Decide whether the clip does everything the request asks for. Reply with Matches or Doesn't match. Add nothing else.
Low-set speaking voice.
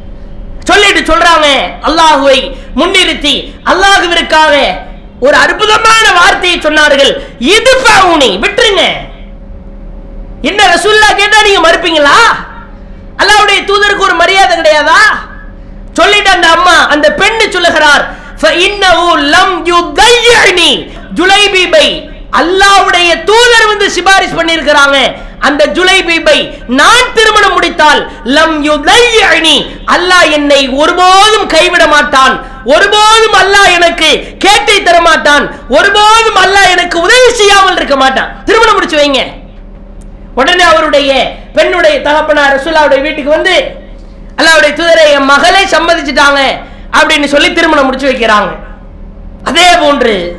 Doesn't match